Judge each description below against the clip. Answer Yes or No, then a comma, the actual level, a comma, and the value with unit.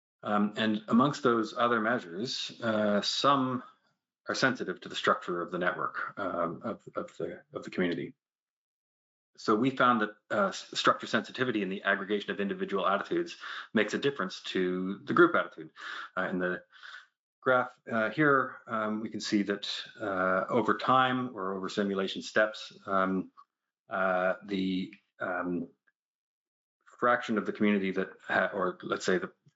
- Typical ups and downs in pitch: Yes, average, 4.5 semitones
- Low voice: Yes, low, 105 Hz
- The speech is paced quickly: No, average, 150 wpm